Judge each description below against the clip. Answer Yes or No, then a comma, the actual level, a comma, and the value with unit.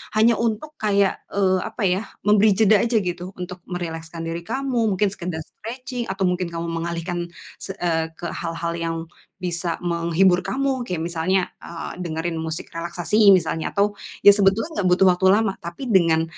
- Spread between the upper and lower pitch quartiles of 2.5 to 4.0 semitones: Yes, average, 3.6 semitones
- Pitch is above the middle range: No, medium, 180 Hz